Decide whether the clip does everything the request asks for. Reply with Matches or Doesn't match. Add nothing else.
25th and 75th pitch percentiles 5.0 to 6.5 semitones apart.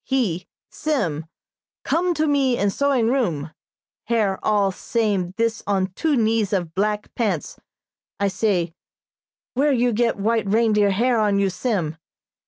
Doesn't match